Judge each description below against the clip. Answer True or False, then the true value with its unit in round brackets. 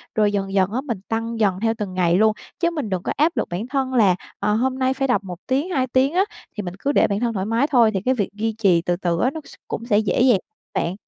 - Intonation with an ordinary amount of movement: True (4.9 semitones)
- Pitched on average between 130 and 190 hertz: False (225 Hz)